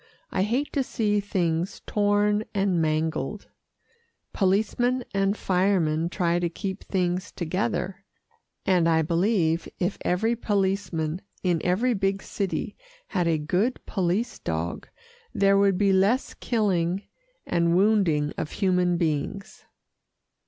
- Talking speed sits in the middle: No, slow, 120 wpm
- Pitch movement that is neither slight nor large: Yes, average, 3.3 semitones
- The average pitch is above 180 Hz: Yes, high, 190 Hz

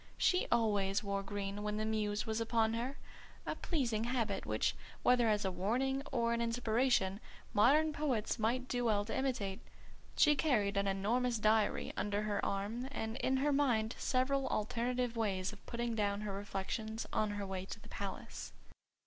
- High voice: Yes, high, 220 Hz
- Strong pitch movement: No, average, 3.3 semitones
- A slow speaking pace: No, average, 170 wpm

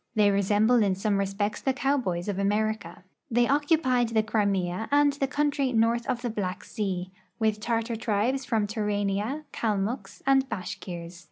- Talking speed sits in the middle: Yes, average, 155 wpm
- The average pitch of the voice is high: Yes, high, 220 Hz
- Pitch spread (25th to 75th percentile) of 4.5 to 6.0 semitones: No, average, 3.8 semitones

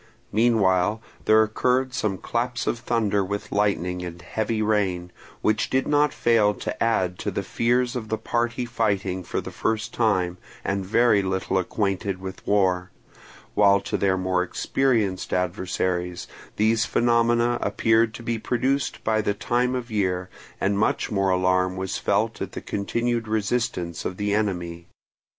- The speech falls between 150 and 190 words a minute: Yes, average, 155 wpm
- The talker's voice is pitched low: Yes, low, 105 Hz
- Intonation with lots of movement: No, average, 3.9 semitones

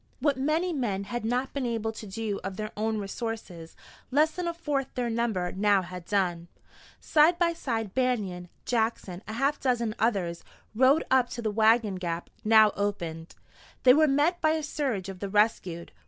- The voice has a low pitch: No, high, 225 Hz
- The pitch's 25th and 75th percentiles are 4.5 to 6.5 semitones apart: Yes, average, 5.2 semitones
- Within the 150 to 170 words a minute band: No, average, 180 wpm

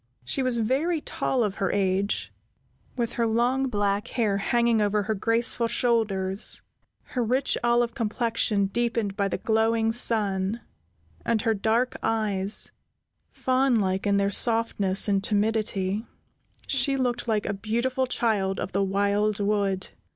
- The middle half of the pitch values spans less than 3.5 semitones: Yes, average, 3.0 semitones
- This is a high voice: Yes, high, 220 Hz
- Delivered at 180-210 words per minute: No, average, 140 wpm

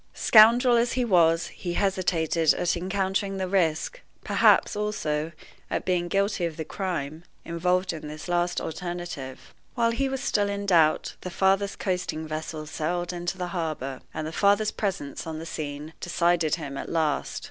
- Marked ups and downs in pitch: No, average, 3.6 semitones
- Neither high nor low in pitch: Yes, medium, 175 Hz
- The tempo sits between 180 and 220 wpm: No, average, 165 wpm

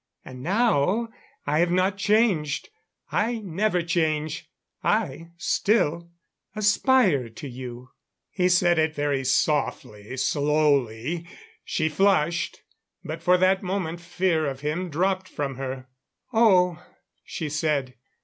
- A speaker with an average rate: No, slow, 115 wpm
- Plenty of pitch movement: No, average, 4.6 semitones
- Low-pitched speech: No, medium, 165 Hz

